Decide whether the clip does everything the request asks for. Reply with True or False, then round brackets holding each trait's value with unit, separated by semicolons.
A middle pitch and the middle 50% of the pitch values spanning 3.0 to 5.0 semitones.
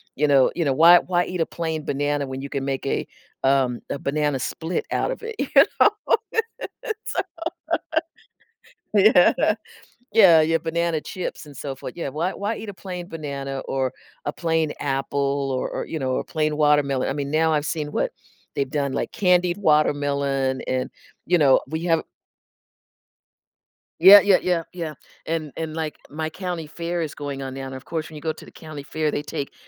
True (155 Hz; 3.3 semitones)